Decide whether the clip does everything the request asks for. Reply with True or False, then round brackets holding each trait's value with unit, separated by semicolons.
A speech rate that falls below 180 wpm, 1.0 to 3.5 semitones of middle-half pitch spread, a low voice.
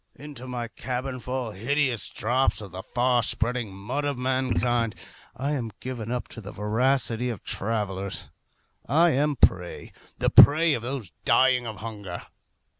True (155 wpm; 3.2 semitones; 125 Hz)